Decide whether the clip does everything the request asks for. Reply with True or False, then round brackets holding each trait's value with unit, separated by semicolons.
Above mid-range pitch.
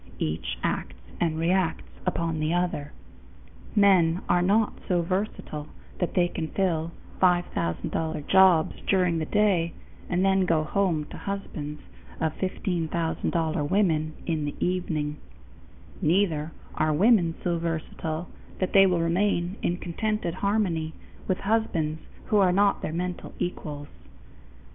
False (175 Hz)